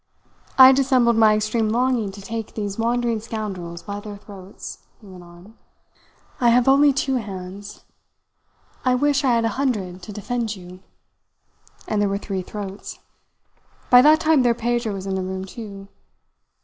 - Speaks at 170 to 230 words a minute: No, average, 160 wpm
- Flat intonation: No, average, 3.8 semitones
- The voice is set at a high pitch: Yes, high, 215 Hz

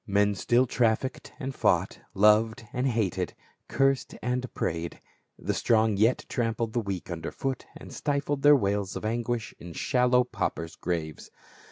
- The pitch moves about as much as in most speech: Yes, average, 4.1 semitones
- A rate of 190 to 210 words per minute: No, average, 150 wpm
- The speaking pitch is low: Yes, low, 115 Hz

